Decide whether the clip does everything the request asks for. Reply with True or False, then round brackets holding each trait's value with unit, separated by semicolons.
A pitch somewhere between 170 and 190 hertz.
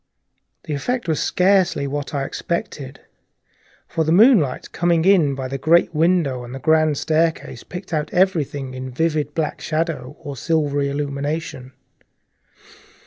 False (155 Hz)